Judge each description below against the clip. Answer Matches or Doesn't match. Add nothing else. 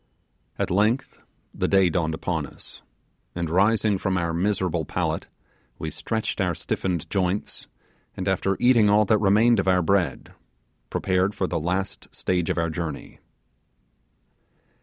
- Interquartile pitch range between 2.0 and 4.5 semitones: Matches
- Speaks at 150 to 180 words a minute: Doesn't match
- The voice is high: Doesn't match